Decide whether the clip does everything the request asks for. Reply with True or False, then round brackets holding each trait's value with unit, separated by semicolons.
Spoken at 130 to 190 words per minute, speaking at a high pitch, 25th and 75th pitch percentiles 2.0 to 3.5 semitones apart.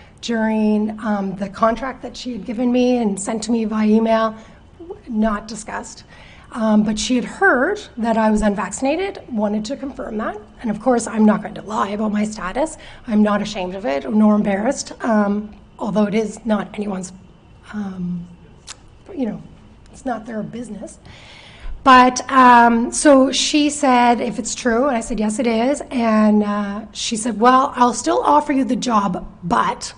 True (175 wpm; 225 Hz; 3.0 semitones)